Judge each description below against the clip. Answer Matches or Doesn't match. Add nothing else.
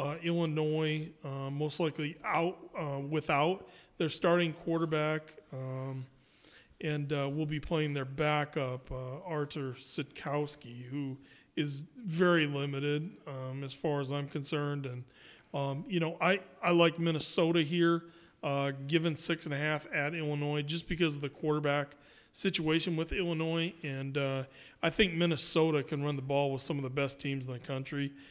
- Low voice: Doesn't match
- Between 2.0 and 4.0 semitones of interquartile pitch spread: Matches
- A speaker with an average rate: Matches